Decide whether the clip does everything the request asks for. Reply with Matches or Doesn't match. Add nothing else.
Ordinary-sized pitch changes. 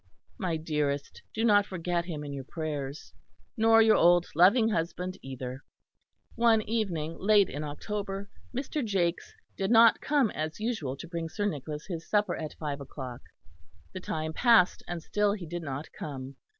Doesn't match